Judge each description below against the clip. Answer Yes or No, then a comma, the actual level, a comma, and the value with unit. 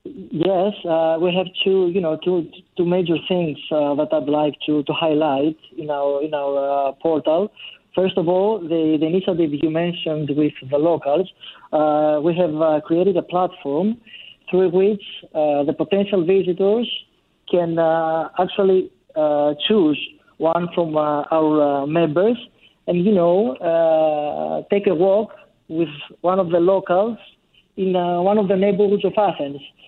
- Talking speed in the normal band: Yes, average, 160 wpm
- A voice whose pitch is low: No, medium, 175 Hz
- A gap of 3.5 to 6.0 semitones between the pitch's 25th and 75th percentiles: Yes, average, 3.8 semitones